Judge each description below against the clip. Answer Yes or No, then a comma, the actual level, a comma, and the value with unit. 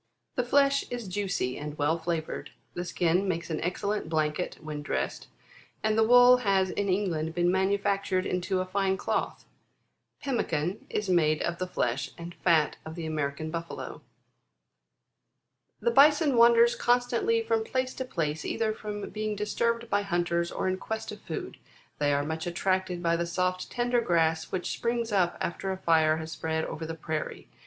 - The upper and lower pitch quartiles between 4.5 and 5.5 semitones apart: Yes, average, 5.0 semitones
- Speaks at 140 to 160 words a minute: No, average, 175 wpm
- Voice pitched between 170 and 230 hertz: Yes, medium, 185 Hz